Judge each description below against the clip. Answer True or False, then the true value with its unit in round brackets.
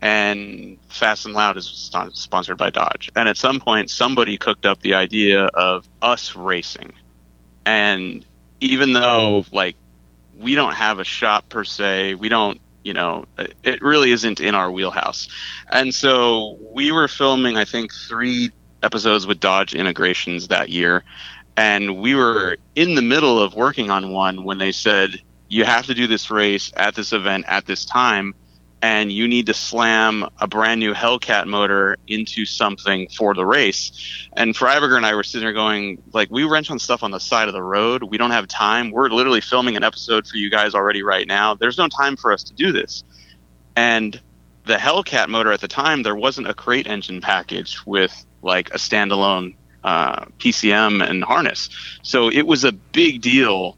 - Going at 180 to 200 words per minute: True (185 wpm)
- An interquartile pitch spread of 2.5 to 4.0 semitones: True (3.5 semitones)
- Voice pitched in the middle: False (105 Hz)